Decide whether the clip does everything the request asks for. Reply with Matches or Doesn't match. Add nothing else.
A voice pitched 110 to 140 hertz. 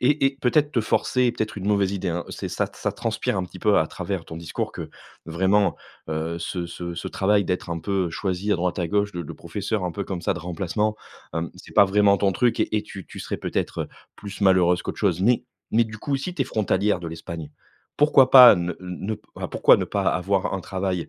Doesn't match